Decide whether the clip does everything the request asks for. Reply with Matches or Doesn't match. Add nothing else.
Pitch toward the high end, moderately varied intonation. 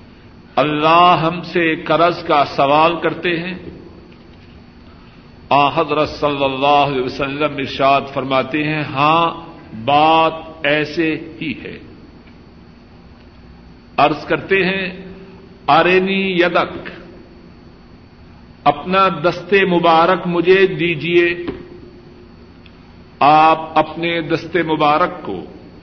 Doesn't match